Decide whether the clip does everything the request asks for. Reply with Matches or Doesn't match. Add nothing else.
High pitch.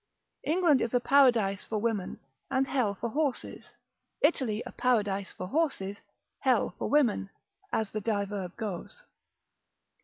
Matches